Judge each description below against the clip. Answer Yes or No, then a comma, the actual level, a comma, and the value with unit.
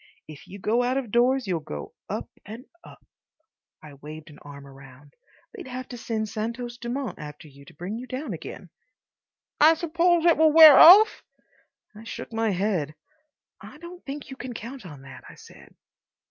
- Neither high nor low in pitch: No, high, 230 Hz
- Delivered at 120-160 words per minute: No, average, 180 wpm